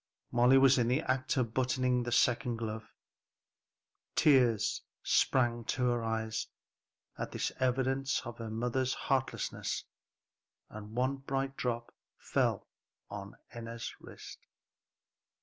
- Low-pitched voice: Yes, low, 125 Hz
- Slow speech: Yes, slow, 115 wpm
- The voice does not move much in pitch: Yes, narrow, 2.3 semitones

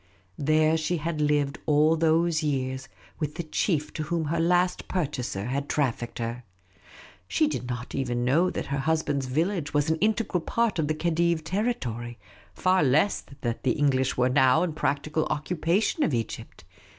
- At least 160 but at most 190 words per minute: Yes, average, 165 wpm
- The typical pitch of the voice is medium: Yes, medium, 150 Hz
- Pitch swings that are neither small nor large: Yes, average, 4.1 semitones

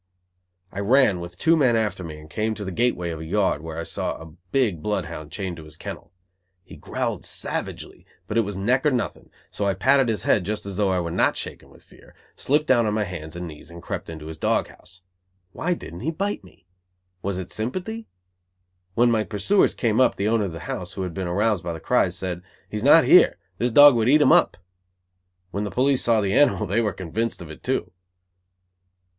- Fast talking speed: Yes, fast, 225 wpm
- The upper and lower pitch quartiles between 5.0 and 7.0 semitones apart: Yes, wide, 5.5 semitones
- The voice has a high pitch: No, low, 100 Hz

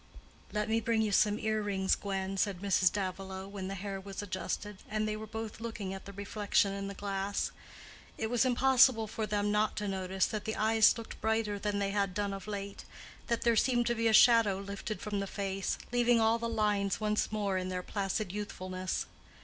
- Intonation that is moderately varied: No, narrow, 2.0 semitones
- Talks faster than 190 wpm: Yes, fast, 205 wpm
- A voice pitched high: Yes, high, 205 Hz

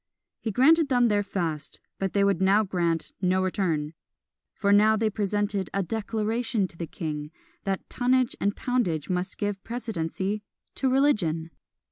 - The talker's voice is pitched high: Yes, high, 200 Hz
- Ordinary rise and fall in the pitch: Yes, average, 3.8 semitones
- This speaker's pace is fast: No, average, 150 wpm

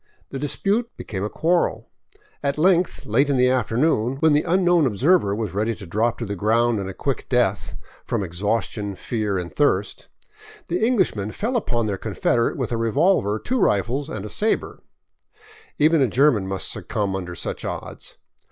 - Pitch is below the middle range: Yes, low, 120 Hz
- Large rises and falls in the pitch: Yes, wide, 6.6 semitones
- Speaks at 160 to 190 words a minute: Yes, average, 175 wpm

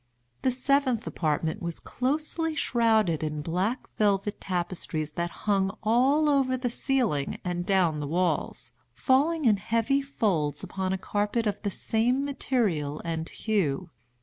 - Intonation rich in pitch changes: Yes, wide, 6.9 semitones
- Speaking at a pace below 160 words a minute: Yes, average, 140 wpm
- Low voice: No, high, 205 Hz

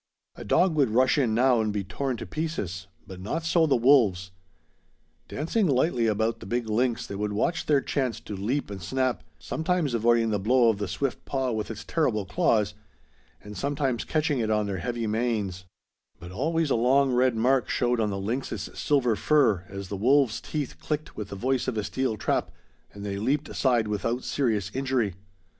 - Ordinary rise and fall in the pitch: Yes, average, 4.5 semitones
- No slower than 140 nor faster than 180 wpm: No, average, 190 wpm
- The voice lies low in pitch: Yes, low, 120 Hz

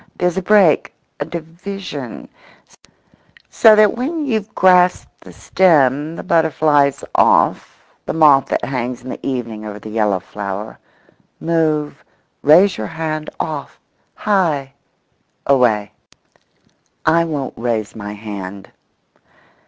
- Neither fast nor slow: No, slow, 105 wpm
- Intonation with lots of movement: Yes, wide, 7.1 semitones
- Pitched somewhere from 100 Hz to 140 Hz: No, medium, 150 Hz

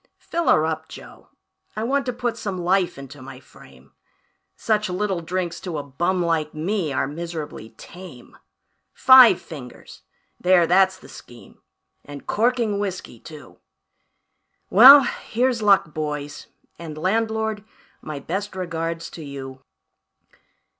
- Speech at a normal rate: No, slow, 130 wpm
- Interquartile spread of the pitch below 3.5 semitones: No, wide, 5.5 semitones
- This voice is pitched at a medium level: Yes, medium, 175 Hz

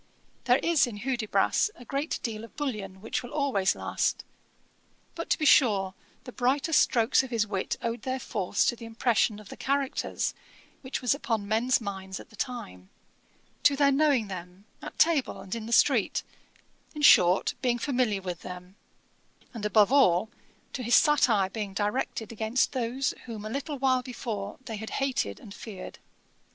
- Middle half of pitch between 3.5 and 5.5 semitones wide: Yes, average, 4.5 semitones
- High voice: Yes, high, 230 Hz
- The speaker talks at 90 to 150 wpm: No, average, 170 wpm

